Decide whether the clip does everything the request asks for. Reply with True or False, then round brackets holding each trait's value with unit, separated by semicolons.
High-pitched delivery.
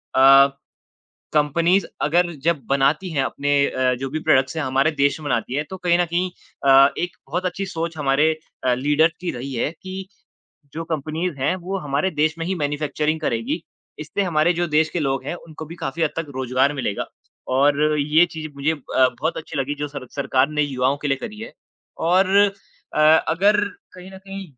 False (150 Hz)